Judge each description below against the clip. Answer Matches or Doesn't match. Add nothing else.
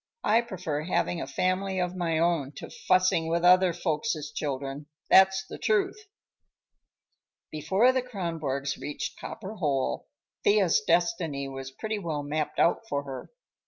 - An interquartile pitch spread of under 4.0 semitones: Doesn't match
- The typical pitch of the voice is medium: Matches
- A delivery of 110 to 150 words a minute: Matches